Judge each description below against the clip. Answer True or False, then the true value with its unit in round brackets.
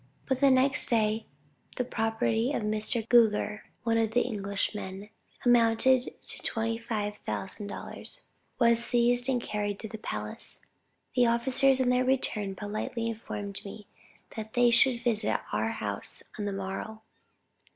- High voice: True (225 Hz)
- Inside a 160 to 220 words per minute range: False (140 wpm)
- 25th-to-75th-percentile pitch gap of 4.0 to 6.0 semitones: False (2.7 semitones)